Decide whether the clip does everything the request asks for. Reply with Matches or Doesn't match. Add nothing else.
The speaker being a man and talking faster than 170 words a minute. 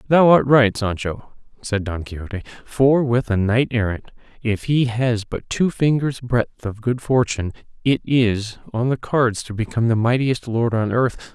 Matches